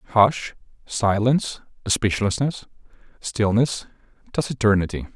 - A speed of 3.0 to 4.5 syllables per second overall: Yes, 4.3 syllables/s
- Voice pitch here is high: No, low, 110 Hz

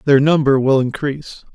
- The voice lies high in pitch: No, medium, 140 Hz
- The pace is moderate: Yes, average, 155 wpm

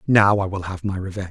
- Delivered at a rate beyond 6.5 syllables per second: Yes, 6.8 syllables/s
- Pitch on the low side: Yes, very low, 95 Hz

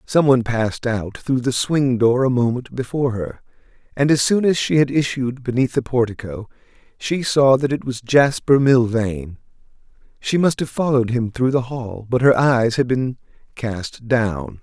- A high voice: No, low, 125 Hz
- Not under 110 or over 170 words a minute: No, average, 180 wpm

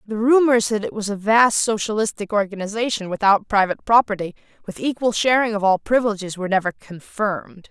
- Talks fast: No, average, 165 wpm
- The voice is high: Yes, high, 210 Hz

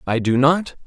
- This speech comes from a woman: No, male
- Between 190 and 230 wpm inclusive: Yes, fast, 210 wpm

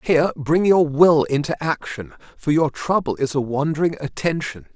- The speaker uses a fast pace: No, average, 165 wpm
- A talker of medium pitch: Yes, medium, 155 Hz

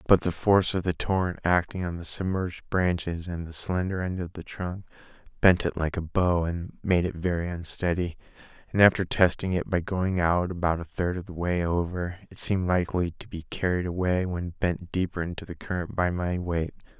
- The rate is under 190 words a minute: No, fast, 205 wpm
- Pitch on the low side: Yes, very low, 90 Hz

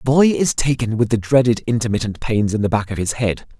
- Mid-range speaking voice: No, low, 115 Hz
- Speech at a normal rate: No, fast, 250 wpm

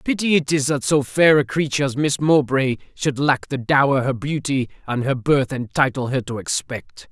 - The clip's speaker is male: Yes, male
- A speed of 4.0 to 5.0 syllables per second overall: Yes, 4.9 syllables/s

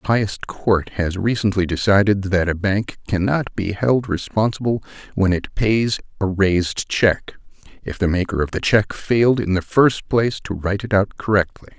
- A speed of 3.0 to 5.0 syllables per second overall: Yes, 4.8 syllables/s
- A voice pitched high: No, low, 100 Hz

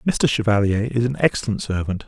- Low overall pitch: Yes, low, 110 Hz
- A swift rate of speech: No, average, 175 wpm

